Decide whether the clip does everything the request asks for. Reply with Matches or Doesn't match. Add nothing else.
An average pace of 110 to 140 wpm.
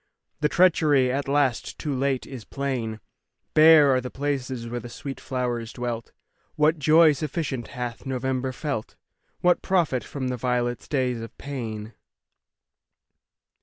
Matches